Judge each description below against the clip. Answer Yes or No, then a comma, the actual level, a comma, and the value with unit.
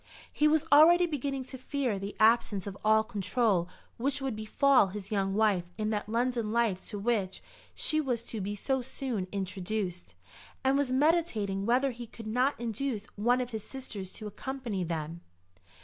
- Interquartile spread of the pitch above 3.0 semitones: Yes, average, 4.7 semitones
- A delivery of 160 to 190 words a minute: Yes, average, 170 wpm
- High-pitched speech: Yes, high, 225 Hz